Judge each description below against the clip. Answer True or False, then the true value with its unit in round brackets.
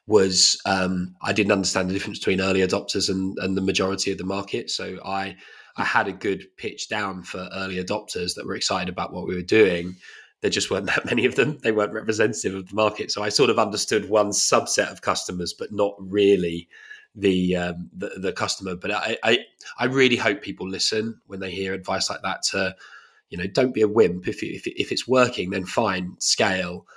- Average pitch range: False (2.0 semitones)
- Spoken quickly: True (215 wpm)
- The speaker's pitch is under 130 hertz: True (95 Hz)